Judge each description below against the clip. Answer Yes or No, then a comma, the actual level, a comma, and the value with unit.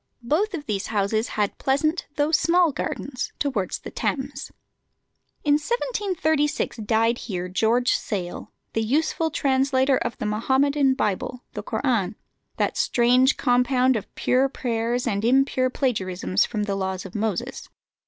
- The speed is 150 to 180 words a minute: No, slow, 135 wpm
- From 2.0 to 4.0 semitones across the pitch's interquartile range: No, average, 4.7 semitones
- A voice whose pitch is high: Yes, very high, 250 Hz